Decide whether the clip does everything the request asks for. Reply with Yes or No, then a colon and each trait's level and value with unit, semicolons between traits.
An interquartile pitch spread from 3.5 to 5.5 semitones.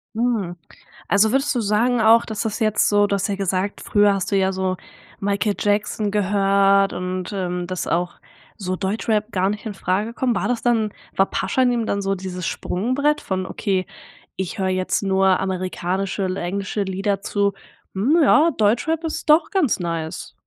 No: average, 2.8 semitones